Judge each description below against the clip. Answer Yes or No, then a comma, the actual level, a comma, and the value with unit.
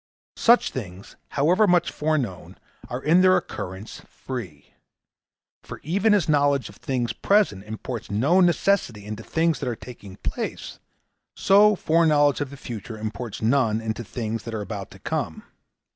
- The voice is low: Yes, low, 125 Hz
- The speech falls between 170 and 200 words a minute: No, average, 150 wpm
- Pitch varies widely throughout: Yes, wide, 7.2 semitones